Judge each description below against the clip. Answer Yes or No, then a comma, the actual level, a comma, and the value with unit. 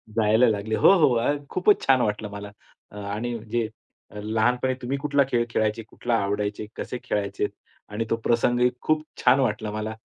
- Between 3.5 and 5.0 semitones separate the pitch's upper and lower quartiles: No, average, 2.9 semitones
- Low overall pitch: Yes, low, 115 Hz